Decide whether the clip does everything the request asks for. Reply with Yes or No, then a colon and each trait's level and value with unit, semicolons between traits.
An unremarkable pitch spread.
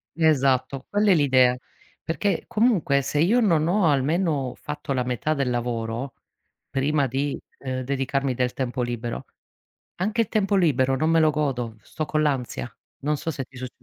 Yes: average, 3.9 semitones